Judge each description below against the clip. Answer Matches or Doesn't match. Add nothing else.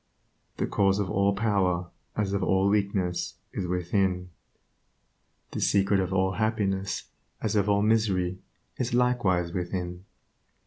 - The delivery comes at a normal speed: Doesn't match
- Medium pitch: Doesn't match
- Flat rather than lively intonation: Matches